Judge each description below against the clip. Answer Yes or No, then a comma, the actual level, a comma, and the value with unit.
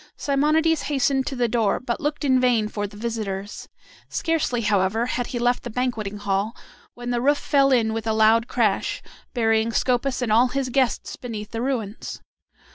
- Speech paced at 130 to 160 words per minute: No, average, 180 wpm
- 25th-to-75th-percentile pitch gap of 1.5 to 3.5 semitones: Yes, average, 3.0 semitones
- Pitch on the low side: No, high, 240 Hz